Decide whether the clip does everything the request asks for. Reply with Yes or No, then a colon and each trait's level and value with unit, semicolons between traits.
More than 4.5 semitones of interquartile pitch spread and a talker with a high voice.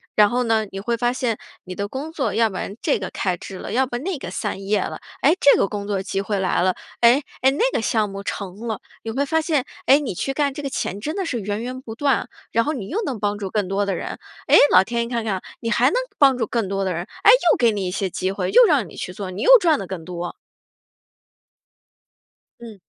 Yes: average, 5.3 semitones; high, 220 Hz